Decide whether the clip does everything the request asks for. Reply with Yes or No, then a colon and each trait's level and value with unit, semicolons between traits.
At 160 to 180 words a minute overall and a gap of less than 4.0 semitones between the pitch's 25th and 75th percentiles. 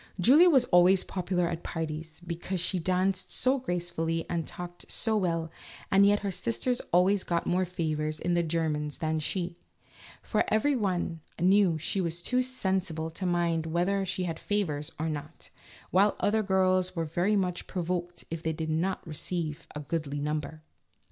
Yes: average, 170 wpm; average, 2.8 semitones